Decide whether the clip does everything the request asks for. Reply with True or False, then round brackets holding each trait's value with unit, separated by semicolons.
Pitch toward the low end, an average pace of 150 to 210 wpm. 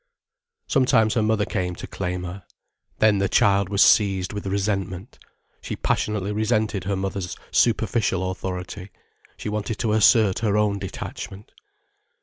False (100 Hz; 135 wpm)